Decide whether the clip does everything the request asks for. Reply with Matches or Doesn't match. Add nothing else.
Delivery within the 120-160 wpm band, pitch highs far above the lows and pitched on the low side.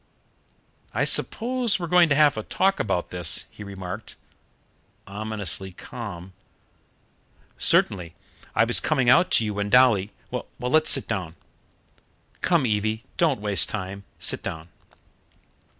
Matches